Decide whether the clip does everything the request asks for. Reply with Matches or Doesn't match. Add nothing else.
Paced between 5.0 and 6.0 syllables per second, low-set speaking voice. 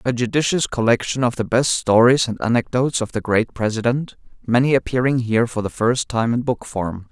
Matches